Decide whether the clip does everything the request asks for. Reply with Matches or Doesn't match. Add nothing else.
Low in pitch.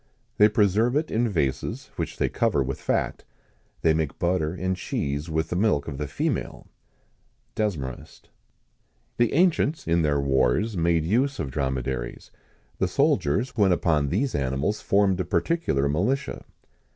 Matches